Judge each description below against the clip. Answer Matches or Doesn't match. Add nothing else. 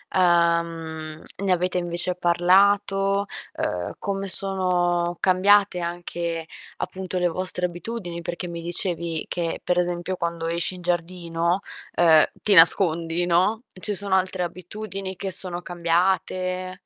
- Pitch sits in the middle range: Matches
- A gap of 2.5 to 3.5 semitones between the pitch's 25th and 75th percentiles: Doesn't match